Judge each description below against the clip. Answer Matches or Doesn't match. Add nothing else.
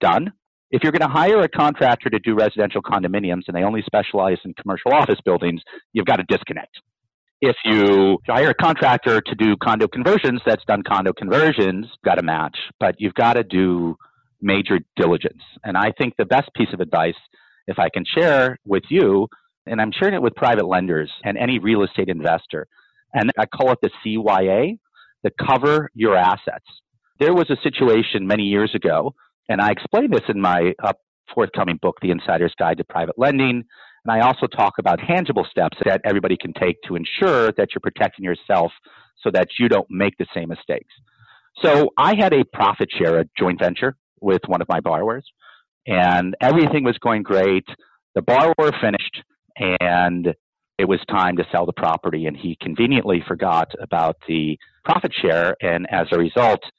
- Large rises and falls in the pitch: Doesn't match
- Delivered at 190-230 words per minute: Doesn't match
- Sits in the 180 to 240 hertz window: Doesn't match